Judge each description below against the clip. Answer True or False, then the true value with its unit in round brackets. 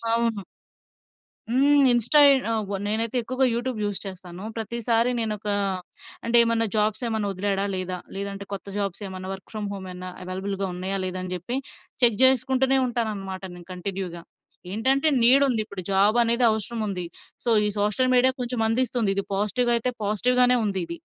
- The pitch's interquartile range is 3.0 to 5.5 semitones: True (3.7 semitones)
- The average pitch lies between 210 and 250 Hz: True (215 Hz)